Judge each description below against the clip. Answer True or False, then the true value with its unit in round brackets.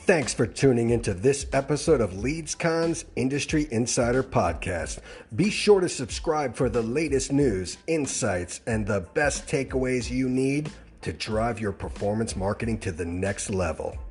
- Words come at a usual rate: True (150 wpm)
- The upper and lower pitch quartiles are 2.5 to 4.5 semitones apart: False (5.3 semitones)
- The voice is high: False (120 Hz)